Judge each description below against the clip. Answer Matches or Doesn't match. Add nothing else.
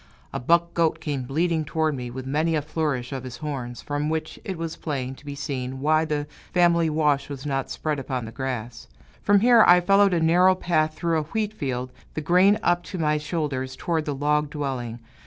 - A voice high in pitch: Doesn't match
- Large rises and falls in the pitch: Doesn't match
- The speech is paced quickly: Matches